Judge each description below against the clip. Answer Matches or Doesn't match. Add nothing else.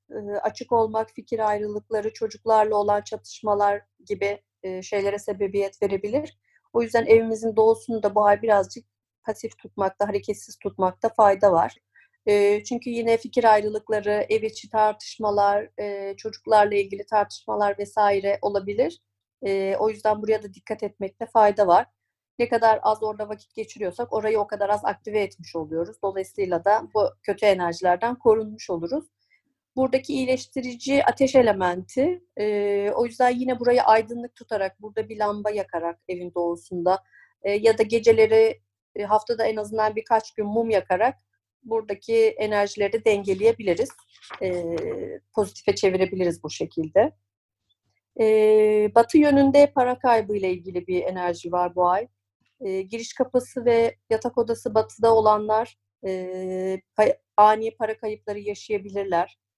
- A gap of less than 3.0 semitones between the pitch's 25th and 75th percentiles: Matches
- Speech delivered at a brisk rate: Doesn't match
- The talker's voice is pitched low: Doesn't match